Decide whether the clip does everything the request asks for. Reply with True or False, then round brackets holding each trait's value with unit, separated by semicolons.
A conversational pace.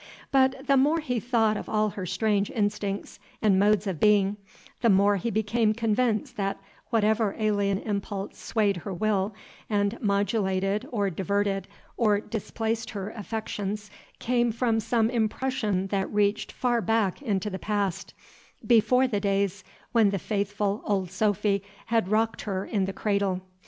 True (150 wpm)